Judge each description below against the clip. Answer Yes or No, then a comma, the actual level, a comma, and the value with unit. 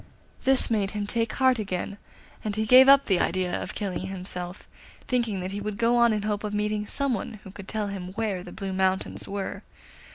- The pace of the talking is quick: Yes, fast, 215 wpm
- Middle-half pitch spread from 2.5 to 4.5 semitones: Yes, average, 2.9 semitones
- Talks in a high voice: Yes, high, 205 Hz